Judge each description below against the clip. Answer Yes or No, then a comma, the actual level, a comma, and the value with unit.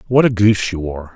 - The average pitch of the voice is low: Yes, low, 100 Hz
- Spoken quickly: Yes, fast, 260 wpm